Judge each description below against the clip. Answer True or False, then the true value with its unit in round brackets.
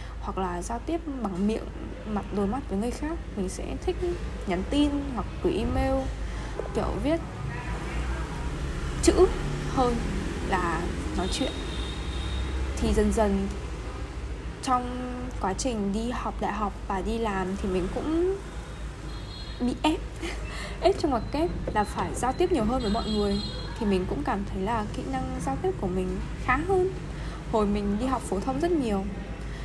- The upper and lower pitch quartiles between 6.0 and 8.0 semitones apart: True (6.7 semitones)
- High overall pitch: True (225 Hz)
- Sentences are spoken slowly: True (160 wpm)